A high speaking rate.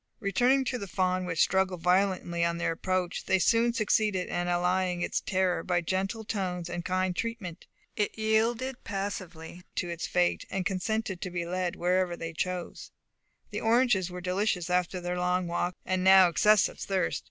No: average, 170 wpm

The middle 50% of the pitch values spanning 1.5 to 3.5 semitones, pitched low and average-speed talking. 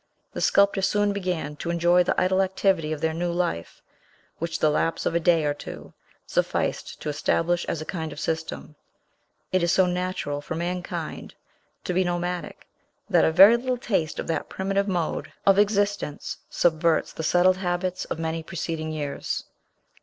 No: average, 2.7 semitones; medium, 175 Hz; average, 170 wpm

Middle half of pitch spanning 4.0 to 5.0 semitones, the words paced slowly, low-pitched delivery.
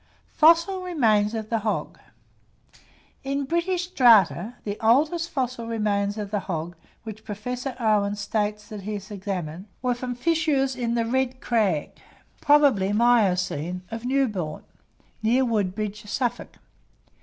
No: average, 4.3 semitones; slow, 130 wpm; high, 225 Hz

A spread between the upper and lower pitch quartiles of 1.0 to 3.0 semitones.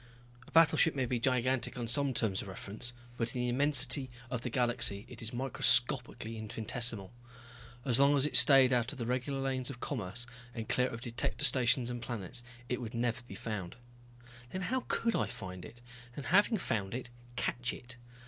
Yes: narrow, 2.4 semitones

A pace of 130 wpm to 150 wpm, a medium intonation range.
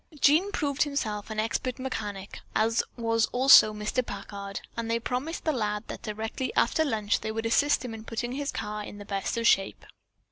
No: average, 190 wpm; average, 3.5 semitones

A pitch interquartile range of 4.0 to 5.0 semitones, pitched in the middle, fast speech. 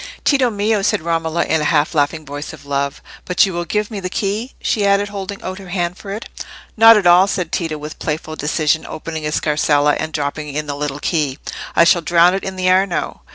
Yes: average, 4.5 semitones; medium, 170 Hz; fast, 225 wpm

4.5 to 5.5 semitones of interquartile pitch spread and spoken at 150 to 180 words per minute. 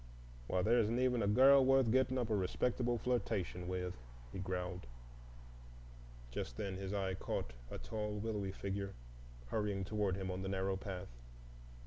No: average, 3.6 semitones; average, 155 wpm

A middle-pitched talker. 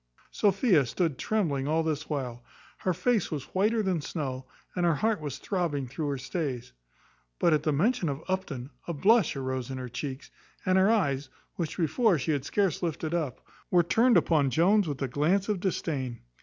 Yes: medium, 160 Hz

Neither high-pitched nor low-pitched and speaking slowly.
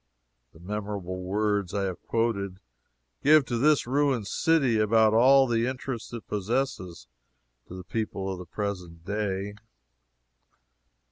No: low, 105 Hz; slow, 125 wpm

